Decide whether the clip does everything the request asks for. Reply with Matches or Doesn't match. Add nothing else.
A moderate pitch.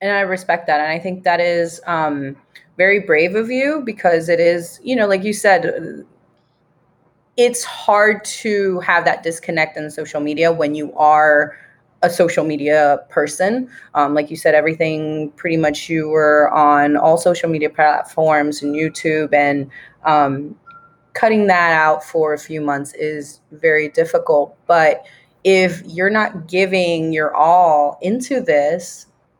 Matches